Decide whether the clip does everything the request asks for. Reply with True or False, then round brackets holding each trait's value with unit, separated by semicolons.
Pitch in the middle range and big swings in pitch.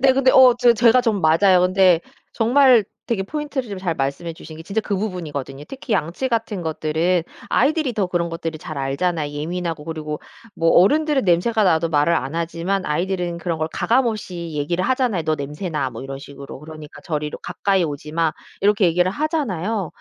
True (180 Hz; 5.8 semitones)